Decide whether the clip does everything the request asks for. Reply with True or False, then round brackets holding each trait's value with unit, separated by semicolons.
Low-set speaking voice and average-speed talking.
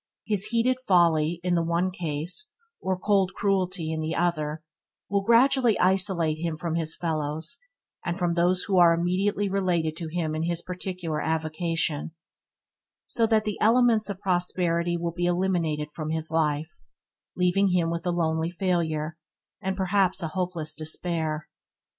False (175 Hz; 155 wpm)